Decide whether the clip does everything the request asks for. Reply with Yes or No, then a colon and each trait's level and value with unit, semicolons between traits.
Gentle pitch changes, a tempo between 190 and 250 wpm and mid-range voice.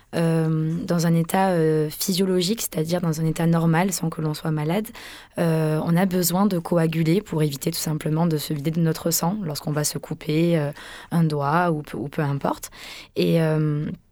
Yes: narrow, 1.7 semitones; average, 195 wpm; medium, 165 Hz